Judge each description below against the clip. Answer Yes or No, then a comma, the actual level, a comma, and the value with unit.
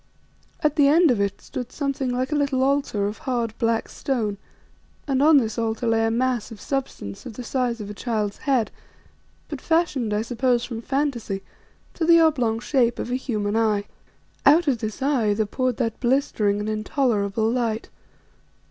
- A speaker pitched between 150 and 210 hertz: No, high, 240 Hz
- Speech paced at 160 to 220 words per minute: Yes, average, 180 wpm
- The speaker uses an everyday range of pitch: Yes, average, 3.8 semitones